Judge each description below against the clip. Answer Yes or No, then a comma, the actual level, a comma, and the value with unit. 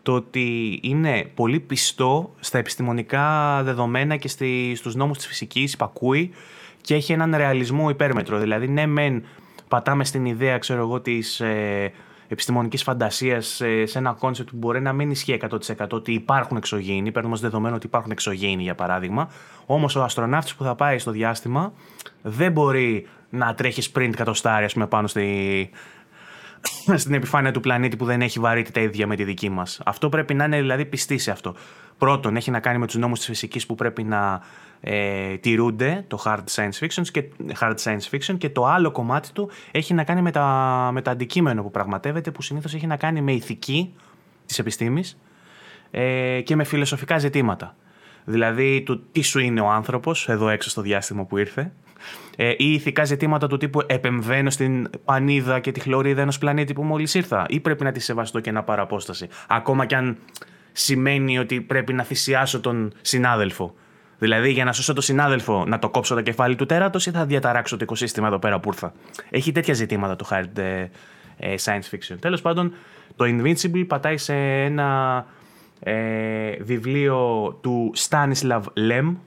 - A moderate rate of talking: No, fast, 175 wpm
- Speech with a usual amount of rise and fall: Yes, average, 4.2 semitones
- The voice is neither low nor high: No, low, 125 Hz